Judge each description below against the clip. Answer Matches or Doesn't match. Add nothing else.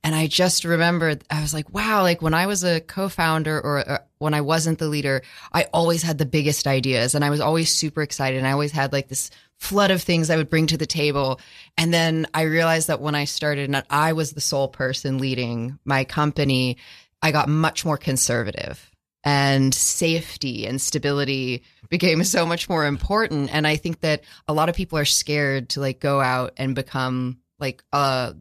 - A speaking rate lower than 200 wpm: Doesn't match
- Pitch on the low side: Doesn't match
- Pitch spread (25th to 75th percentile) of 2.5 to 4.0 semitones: Matches